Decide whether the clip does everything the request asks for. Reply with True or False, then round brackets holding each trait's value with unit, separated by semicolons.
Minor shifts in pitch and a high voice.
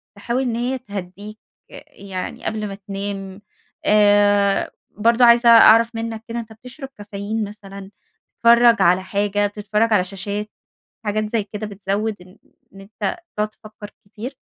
True (2.2 semitones; 210 Hz)